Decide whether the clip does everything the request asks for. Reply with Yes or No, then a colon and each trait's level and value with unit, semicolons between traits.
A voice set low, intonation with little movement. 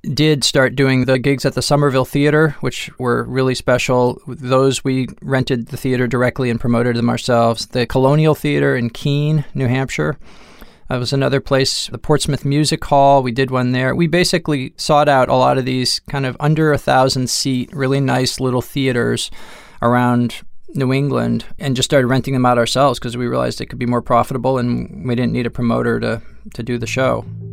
Yes: low, 130 Hz; narrow, 2.1 semitones